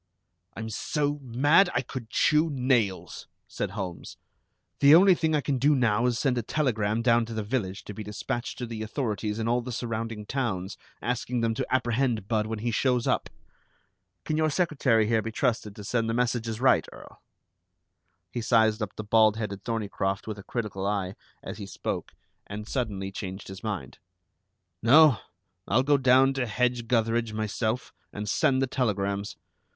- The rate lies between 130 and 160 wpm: No, average, 175 wpm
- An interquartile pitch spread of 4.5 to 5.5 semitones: No, average, 3.2 semitones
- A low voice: Yes, low, 115 Hz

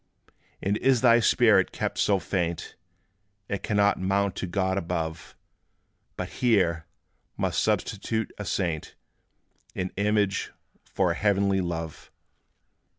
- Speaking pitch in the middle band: No, very low, 95 Hz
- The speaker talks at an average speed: No, slow, 115 wpm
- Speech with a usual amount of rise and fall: Yes, average, 3.0 semitones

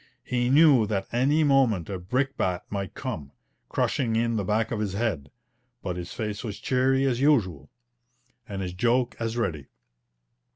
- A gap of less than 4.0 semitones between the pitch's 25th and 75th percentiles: No, average, 5.1 semitones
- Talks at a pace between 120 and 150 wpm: No, average, 160 wpm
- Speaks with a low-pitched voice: Yes, low, 110 Hz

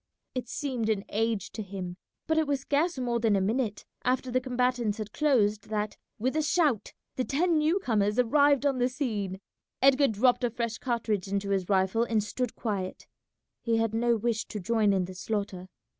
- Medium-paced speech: Yes, average, 190 wpm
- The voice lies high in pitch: Yes, high, 230 Hz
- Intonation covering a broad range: No, average, 3.8 semitones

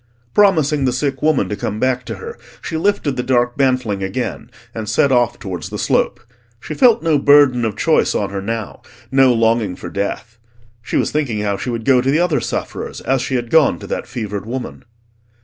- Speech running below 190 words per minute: No, fast, 205 wpm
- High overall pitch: No, low, 125 Hz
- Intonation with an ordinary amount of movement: Yes, average, 4.2 semitones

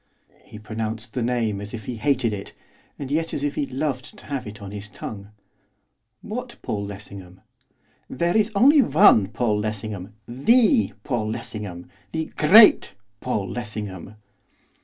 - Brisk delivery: No, average, 150 wpm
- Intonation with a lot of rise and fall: Yes, wide, 5.8 semitones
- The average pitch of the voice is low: Yes, low, 115 Hz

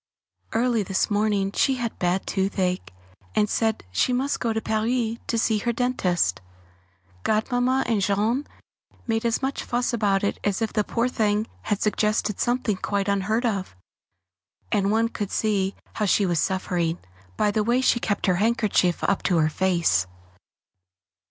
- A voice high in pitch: Yes, high, 210 Hz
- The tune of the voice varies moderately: Yes, average, 3.1 semitones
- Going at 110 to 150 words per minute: No, average, 160 wpm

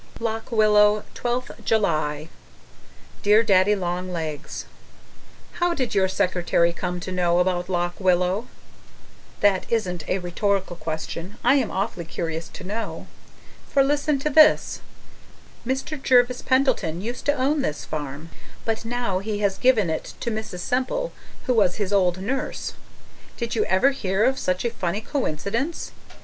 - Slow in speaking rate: No, average, 145 wpm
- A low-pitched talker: No, high, 205 Hz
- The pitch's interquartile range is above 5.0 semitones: Yes, wide, 5.4 semitones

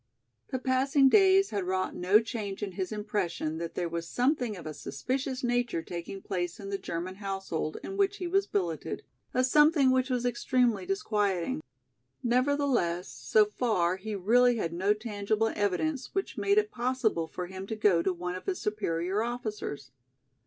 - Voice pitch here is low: No, high, 215 Hz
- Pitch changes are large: Yes, wide, 5.8 semitones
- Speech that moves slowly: No, average, 170 wpm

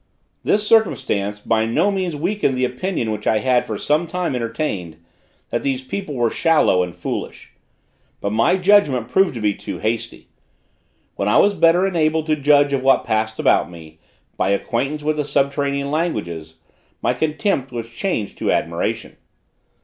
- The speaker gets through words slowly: No, average, 165 wpm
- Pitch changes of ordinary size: No, wide, 6.7 semitones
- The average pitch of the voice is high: No, low, 135 Hz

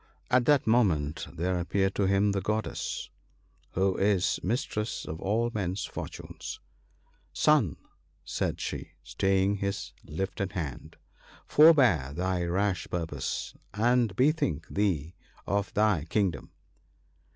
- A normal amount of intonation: Yes, average, 3.5 semitones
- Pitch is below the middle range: Yes, very low, 95 Hz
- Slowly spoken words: Yes, slow, 125 wpm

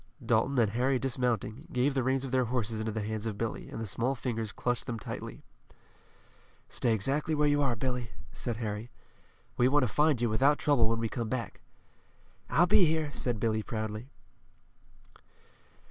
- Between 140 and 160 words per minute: No, average, 175 wpm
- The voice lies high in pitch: No, low, 120 Hz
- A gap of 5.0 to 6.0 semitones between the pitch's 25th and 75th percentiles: No, average, 3.2 semitones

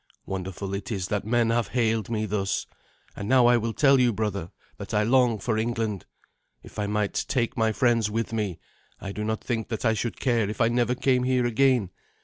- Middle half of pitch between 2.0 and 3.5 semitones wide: Yes, narrow, 2.6 semitones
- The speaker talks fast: Yes, fast, 210 wpm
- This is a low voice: Yes, low, 110 Hz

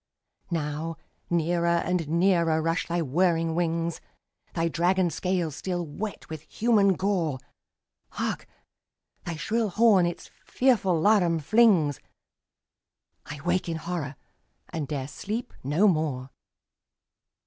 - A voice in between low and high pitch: Yes, medium, 170 Hz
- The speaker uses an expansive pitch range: No, average, 2.9 semitones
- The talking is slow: Yes, slow, 115 wpm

